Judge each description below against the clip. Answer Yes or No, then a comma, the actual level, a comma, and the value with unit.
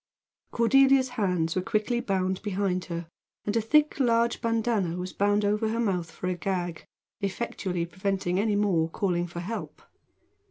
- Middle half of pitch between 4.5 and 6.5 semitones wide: No, average, 4.1 semitones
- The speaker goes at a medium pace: Yes, average, 155 wpm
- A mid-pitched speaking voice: No, high, 200 Hz